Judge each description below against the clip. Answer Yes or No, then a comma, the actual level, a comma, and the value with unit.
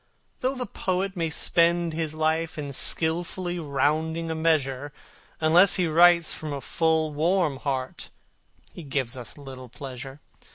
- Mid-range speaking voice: Yes, medium, 160 Hz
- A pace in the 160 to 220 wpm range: No, average, 140 wpm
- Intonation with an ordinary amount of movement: Yes, average, 3.3 semitones